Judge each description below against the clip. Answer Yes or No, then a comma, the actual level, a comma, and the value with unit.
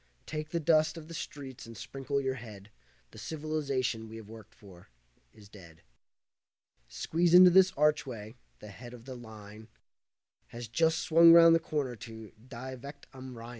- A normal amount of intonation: No, wide, 5.8 semitones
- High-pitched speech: No, low, 130 Hz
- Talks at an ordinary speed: Yes, average, 165 wpm